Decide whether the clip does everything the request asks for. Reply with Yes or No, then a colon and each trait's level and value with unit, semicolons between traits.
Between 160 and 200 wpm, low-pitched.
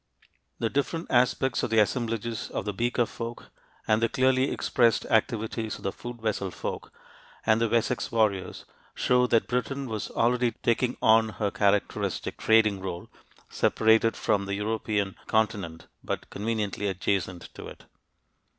No: average, 145 wpm; low, 110 Hz